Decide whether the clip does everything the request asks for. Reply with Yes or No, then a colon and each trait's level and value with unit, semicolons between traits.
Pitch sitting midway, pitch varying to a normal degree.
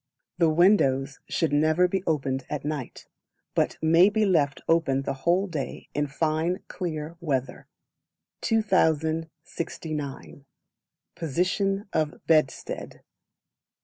Yes: medium, 160 Hz; average, 3.5 semitones